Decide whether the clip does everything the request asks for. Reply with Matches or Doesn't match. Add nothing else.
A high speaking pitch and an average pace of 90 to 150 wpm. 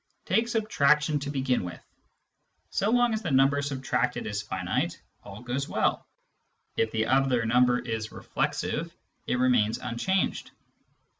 Doesn't match